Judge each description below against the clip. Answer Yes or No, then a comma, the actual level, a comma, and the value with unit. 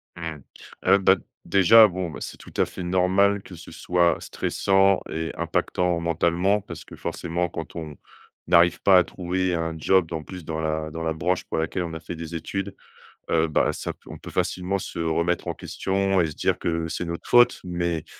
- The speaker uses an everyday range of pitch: No, narrow, 2.2 semitones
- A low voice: Yes, very low, 85 Hz